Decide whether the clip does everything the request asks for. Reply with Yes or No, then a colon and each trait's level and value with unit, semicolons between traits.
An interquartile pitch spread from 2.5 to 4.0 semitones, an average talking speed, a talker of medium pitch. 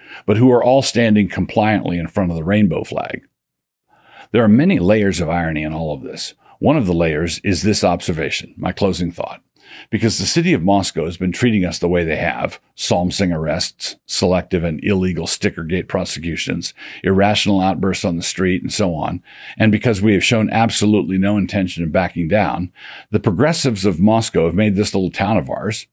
No: average, 3.3 semitones; average, 190 wpm; low, 100 Hz